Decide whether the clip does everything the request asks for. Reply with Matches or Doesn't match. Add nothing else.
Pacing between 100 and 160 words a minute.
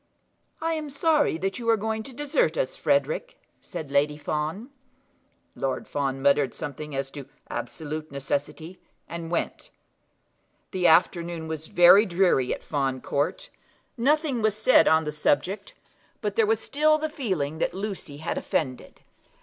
Matches